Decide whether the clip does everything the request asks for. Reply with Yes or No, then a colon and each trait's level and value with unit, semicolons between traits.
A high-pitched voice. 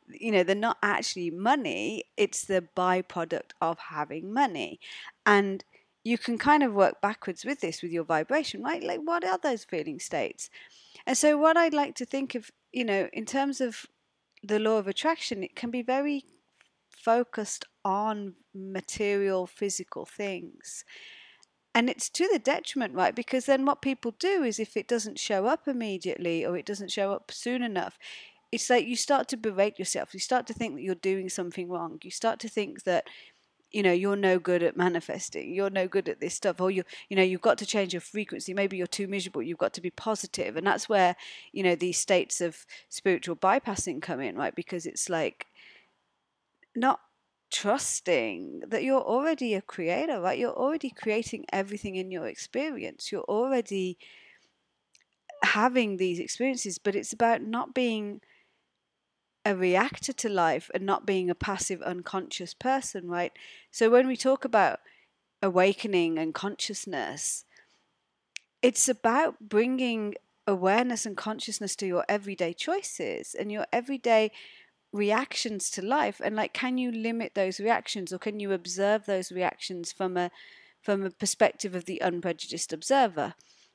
Yes: high, 210 Hz